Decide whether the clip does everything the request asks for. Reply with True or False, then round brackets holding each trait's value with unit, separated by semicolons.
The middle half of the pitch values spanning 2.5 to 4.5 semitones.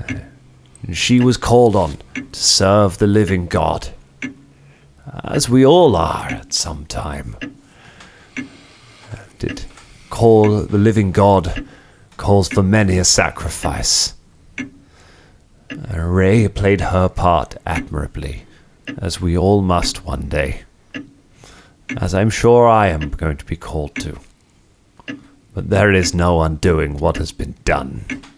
True (3.6 semitones)